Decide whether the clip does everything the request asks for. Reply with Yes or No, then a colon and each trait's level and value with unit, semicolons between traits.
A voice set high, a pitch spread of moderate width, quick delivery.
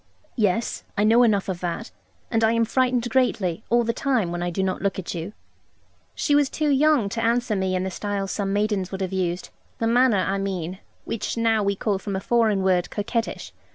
Yes: high, 205 Hz; average, 3.5 semitones; fast, 215 wpm